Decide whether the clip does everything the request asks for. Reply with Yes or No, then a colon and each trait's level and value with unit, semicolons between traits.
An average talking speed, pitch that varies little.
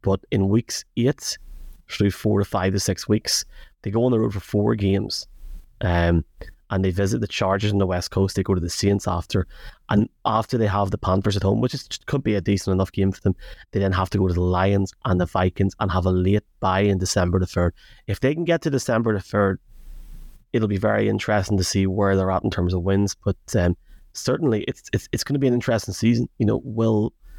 No: fast, 240 wpm; narrow, 2.3 semitones